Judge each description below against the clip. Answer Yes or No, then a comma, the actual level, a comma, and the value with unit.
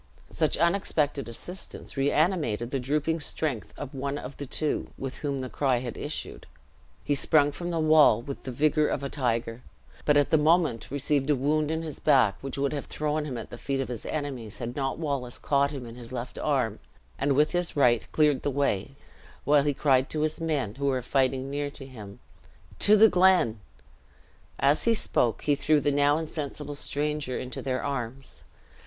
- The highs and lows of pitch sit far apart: No, average, 2.8 semitones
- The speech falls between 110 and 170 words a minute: No, average, 190 wpm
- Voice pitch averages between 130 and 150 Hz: Yes, medium, 140 Hz